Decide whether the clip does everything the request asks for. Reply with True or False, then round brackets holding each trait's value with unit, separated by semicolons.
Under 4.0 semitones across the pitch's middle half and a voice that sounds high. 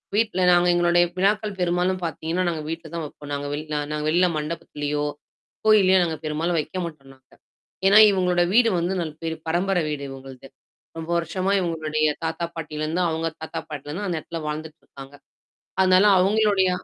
False (3.3 semitones; 165 Hz)